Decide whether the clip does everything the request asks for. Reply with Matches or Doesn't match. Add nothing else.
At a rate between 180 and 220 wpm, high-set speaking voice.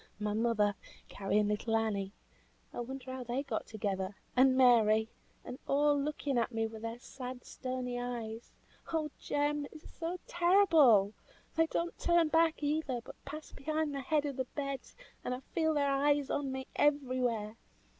Doesn't match